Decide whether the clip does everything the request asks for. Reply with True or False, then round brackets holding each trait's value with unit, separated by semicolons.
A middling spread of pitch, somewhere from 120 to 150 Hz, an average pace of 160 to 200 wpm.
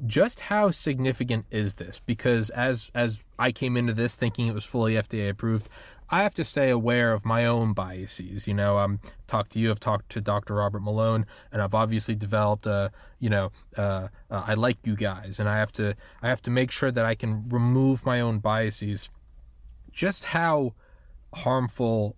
False (3.0 semitones; 110 Hz; 190 wpm)